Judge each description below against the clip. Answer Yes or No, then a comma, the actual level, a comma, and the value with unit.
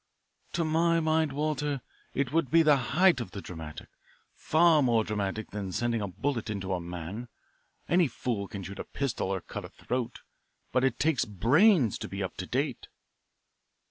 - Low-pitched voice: Yes, low, 125 Hz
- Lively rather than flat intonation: Yes, wide, 7.4 semitones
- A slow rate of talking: No, average, 175 wpm